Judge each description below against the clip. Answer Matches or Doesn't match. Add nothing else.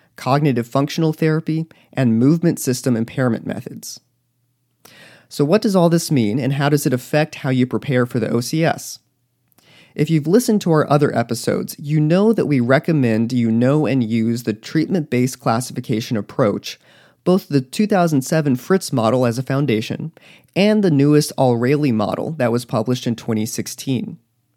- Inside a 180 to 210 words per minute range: Doesn't match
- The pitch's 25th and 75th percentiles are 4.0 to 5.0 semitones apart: Matches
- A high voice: Doesn't match